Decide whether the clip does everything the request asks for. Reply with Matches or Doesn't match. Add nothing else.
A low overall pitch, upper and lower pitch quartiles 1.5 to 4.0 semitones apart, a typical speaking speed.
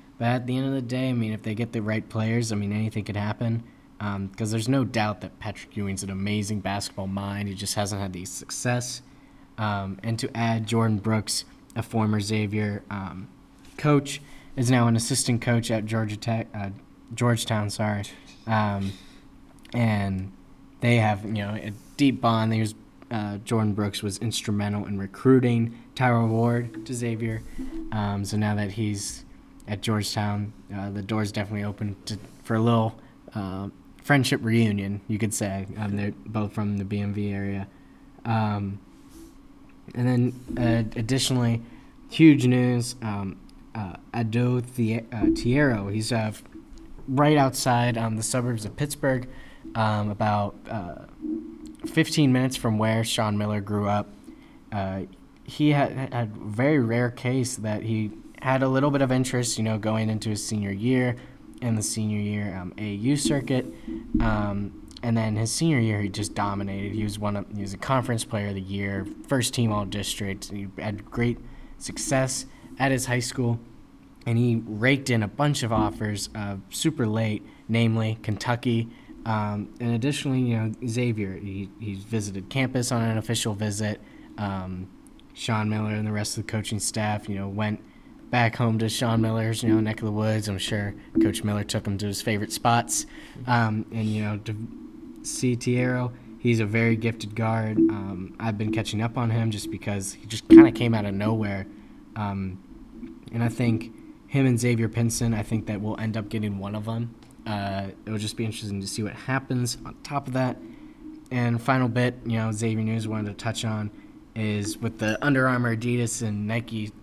Matches